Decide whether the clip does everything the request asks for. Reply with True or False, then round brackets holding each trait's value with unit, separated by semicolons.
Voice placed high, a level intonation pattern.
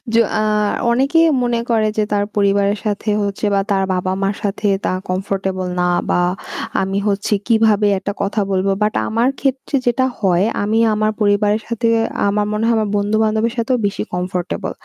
True (205 Hz; 2.2 semitones)